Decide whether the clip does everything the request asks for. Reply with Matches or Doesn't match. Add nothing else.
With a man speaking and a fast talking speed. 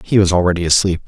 Matches